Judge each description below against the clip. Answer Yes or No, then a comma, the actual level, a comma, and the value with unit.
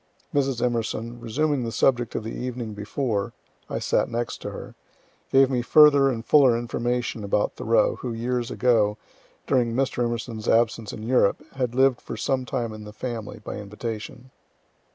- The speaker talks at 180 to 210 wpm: No, average, 165 wpm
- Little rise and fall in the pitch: Yes, narrow, 2.2 semitones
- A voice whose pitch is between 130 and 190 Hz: No, low, 120 Hz